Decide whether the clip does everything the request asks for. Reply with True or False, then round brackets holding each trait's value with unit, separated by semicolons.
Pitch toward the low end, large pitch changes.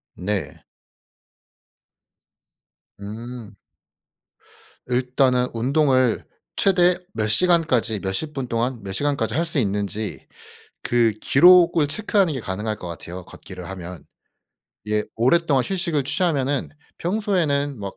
True (130 Hz; 7.0 semitones)